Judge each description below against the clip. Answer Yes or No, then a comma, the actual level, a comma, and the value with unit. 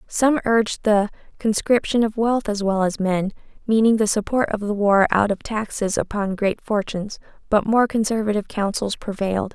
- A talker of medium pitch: No, high, 210 Hz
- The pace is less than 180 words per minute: Yes, average, 170 wpm